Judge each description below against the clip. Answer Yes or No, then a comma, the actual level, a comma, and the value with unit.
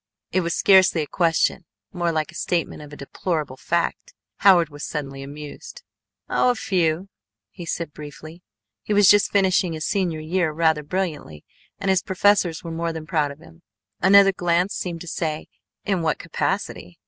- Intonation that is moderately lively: Yes, average, 3.3 semitones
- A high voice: No, medium, 170 Hz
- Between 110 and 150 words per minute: No, average, 170 wpm